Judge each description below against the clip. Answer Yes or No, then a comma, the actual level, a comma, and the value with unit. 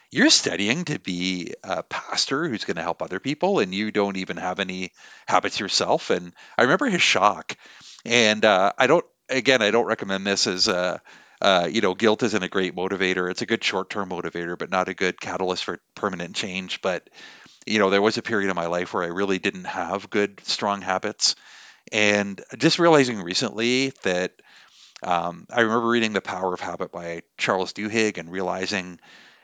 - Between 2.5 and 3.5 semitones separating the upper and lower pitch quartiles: Yes, average, 3.0 semitones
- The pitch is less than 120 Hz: Yes, very low, 95 Hz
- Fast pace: No, average, 190 wpm